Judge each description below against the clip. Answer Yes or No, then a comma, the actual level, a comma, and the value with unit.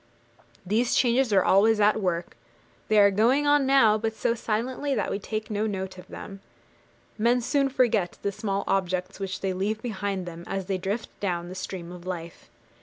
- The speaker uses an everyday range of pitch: Yes, average, 3.4 semitones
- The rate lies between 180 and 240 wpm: Yes, average, 185 wpm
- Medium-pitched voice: No, high, 205 Hz